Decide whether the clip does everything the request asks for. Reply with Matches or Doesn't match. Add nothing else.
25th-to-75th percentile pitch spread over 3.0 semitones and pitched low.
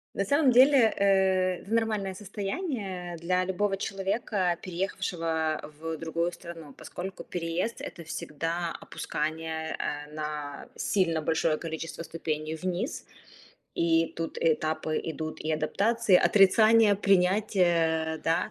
Doesn't match